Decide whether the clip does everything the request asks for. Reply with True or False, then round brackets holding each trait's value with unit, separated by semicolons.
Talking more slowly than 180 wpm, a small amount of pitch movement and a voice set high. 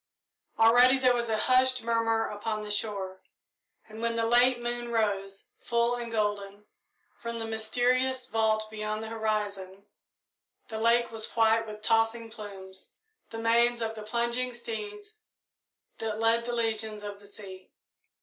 True (150 wpm; 1.9 semitones; 225 Hz)